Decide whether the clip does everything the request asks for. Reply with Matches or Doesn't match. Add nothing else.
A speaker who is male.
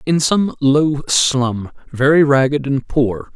Matches